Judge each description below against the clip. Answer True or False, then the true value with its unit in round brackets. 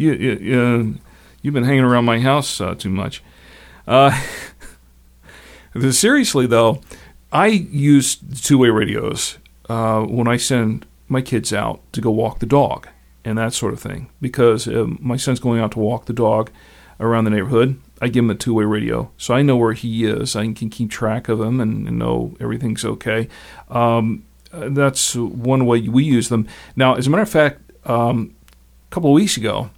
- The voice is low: True (115 Hz)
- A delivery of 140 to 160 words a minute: False (185 wpm)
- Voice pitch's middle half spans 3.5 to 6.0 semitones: False (3.0 semitones)